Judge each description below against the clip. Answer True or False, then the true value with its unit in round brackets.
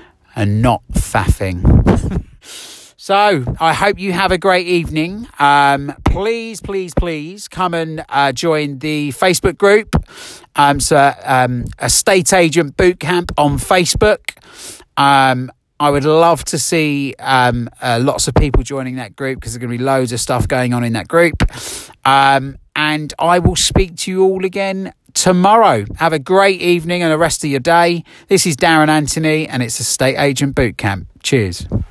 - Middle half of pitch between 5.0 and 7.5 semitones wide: True (5.5 semitones)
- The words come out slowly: False (165 wpm)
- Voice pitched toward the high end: False (150 Hz)